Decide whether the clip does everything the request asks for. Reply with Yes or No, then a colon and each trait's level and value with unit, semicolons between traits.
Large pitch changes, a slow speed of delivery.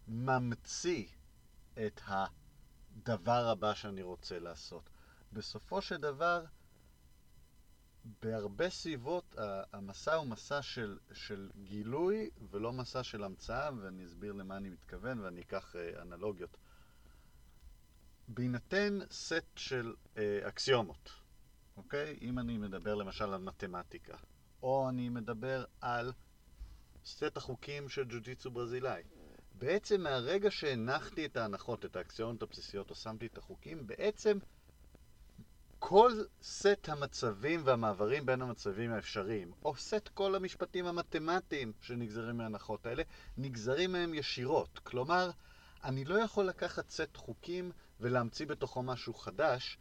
Yes: wide, 6.6 semitones; slow, 110 wpm